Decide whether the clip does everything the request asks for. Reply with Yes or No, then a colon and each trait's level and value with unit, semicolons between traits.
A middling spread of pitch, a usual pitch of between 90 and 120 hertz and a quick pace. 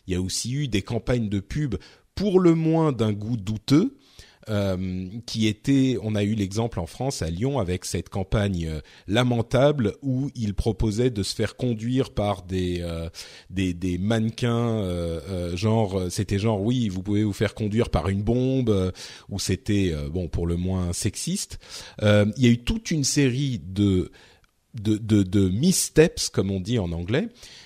No: average, 4.4 semitones; low, 105 Hz; average, 180 wpm